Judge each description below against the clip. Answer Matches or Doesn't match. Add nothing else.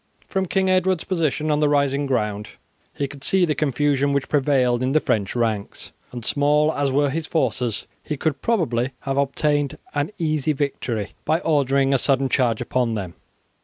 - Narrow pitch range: Doesn't match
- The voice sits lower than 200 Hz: Matches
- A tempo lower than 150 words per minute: Doesn't match